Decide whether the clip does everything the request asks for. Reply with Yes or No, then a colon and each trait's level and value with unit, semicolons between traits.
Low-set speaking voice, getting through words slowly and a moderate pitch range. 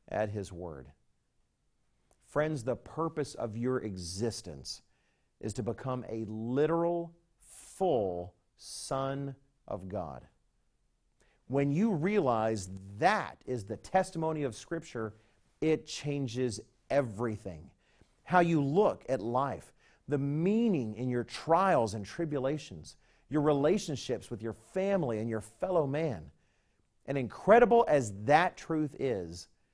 No: low, 125 Hz; slow, 115 wpm; wide, 5.9 semitones